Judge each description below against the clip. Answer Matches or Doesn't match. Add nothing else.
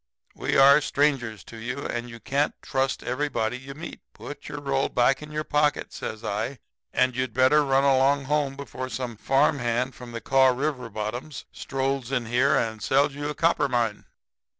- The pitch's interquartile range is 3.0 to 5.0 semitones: Doesn't match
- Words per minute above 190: Doesn't match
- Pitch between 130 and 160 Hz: Matches